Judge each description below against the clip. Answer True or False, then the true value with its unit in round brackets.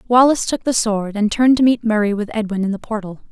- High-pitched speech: True (220 Hz)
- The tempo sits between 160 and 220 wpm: False (255 wpm)